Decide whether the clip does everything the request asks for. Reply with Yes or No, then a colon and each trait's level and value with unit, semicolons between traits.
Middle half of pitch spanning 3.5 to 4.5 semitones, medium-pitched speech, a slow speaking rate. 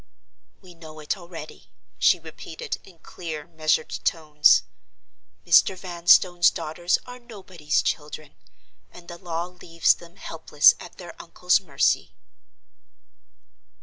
No: narrow, 2.4 semitones; medium, 170 Hz; slow, 115 wpm